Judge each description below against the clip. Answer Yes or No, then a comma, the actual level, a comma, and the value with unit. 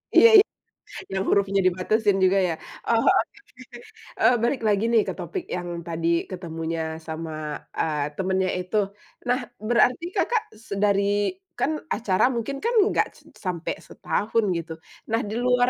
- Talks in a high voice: Yes, high, 200 Hz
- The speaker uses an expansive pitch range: Yes, wide, 5.7 semitones